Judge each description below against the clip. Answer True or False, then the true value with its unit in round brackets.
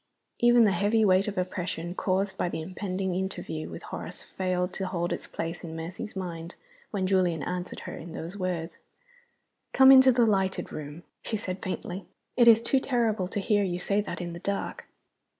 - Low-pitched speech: False (185 Hz)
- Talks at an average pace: True (185 wpm)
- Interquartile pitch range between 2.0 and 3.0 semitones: True (2.7 semitones)